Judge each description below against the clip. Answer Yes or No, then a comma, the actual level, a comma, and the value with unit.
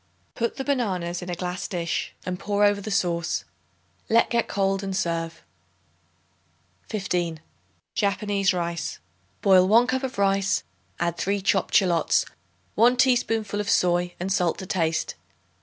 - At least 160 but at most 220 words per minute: No, average, 140 wpm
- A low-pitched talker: No, high, 195 Hz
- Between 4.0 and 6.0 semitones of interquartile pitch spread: No, average, 2.8 semitones